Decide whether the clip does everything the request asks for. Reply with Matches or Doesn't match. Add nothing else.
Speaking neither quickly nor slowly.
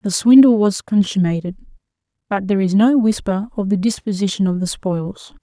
Matches